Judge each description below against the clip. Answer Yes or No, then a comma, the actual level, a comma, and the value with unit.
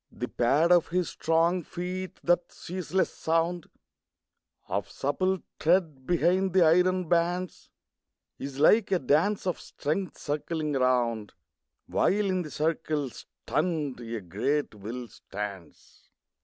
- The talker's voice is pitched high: No, medium, 165 Hz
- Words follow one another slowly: Yes, slow, 120 wpm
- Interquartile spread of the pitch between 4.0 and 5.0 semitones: Yes, average, 4.7 semitones